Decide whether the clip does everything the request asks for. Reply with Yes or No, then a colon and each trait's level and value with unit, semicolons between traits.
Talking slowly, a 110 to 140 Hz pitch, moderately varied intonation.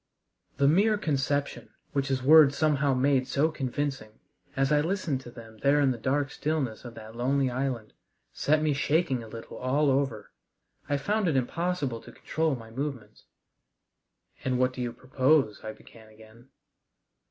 No: average, 165 wpm; low, 135 Hz; average, 3.1 semitones